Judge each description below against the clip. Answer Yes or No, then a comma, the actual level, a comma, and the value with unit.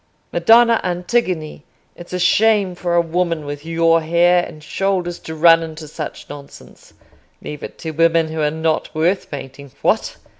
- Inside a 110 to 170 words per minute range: Yes, average, 155 wpm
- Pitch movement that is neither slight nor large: No, narrow, 2.2 semitones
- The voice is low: No, medium, 165 Hz